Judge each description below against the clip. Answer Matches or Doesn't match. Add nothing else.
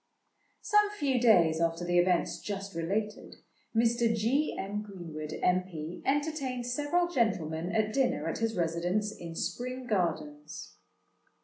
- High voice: Matches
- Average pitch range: Doesn't match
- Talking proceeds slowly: Matches